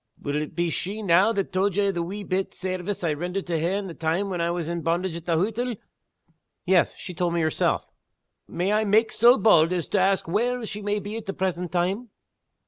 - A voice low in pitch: No, medium, 185 Hz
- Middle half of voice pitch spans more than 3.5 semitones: No, average, 3.1 semitones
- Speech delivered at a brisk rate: Yes, fast, 230 wpm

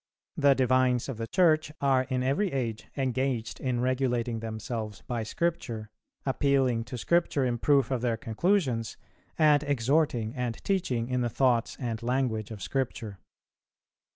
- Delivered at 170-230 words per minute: No, average, 145 wpm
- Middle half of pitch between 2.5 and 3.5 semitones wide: Yes, average, 3.1 semitones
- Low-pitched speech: Yes, low, 125 Hz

